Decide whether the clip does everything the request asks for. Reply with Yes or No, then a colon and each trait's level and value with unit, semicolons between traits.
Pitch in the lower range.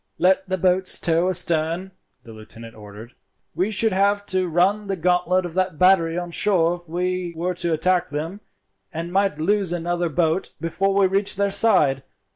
No: medium, 180 Hz